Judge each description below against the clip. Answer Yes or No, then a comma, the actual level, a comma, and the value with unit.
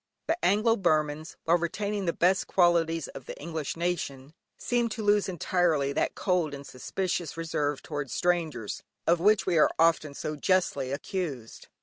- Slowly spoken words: No, average, 155 wpm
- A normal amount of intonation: Yes, average, 4.0 semitones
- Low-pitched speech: No, medium, 165 Hz